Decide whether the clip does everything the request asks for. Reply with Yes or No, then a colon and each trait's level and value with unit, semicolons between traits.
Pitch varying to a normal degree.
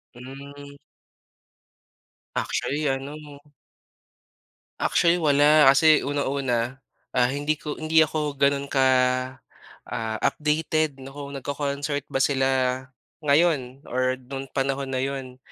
No: narrow, 1.7 semitones